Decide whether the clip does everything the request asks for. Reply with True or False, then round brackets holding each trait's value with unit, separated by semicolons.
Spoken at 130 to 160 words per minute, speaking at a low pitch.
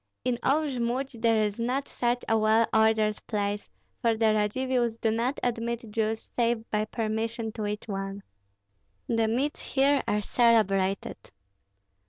False (145 wpm; 225 Hz)